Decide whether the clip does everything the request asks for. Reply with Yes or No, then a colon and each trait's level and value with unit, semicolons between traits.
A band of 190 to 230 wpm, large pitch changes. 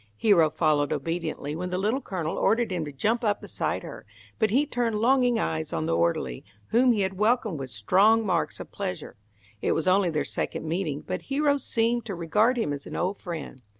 Yes: fast, 205 wpm; wide, 6.6 semitones